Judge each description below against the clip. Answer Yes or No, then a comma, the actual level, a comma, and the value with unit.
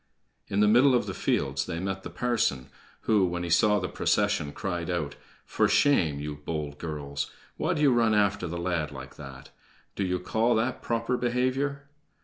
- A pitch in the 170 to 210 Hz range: No, very low, 90 Hz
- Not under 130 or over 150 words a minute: No, average, 185 wpm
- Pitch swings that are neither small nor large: No, wide, 7.6 semitones